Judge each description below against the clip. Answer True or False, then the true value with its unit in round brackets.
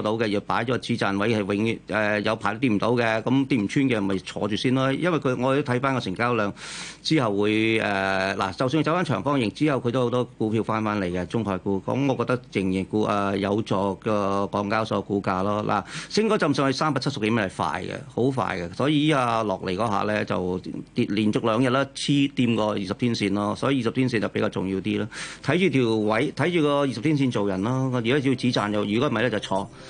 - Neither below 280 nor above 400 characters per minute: True (345 characters per minute)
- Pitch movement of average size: True (4.6 semitones)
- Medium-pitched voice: False (110 Hz)